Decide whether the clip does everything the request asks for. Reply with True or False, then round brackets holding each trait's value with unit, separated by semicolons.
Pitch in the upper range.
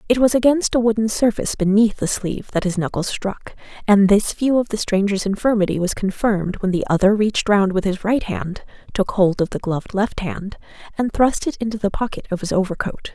True (205 Hz)